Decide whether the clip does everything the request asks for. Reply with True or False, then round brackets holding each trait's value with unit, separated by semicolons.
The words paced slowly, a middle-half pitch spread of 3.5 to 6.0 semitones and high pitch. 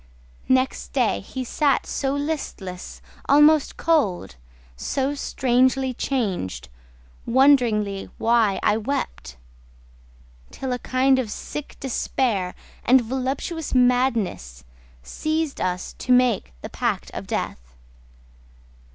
True (100 wpm; 4.6 semitones; 255 Hz)